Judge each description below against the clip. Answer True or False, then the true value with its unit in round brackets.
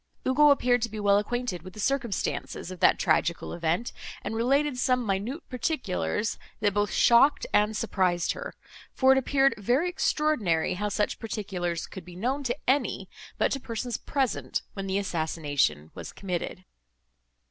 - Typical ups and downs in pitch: False (5.8 semitones)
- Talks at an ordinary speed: True (160 wpm)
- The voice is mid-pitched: False (215 Hz)